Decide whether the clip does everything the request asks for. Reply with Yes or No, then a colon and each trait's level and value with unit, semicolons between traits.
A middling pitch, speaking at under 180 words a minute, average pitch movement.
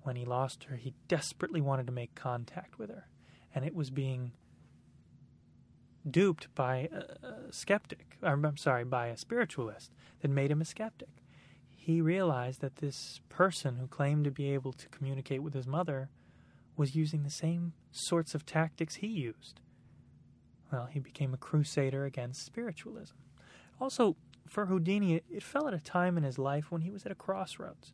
Yes: medium, 145 Hz; average, 170 wpm; average, 4.1 semitones